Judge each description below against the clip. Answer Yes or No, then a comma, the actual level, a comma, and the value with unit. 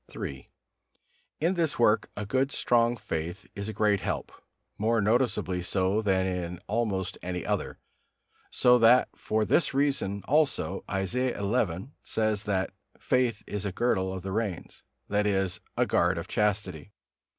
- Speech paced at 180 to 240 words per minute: No, average, 150 wpm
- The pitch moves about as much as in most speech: Yes, average, 3.9 semitones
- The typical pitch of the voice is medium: No, low, 105 Hz